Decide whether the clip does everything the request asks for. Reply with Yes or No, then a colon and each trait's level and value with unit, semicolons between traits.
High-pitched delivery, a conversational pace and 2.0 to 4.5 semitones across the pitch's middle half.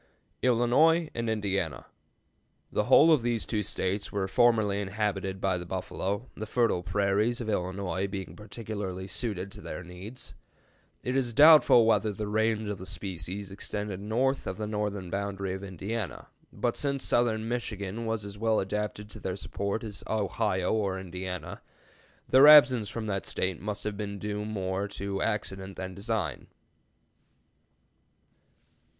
No: low, 105 Hz; average, 150 wpm; average, 2.8 semitones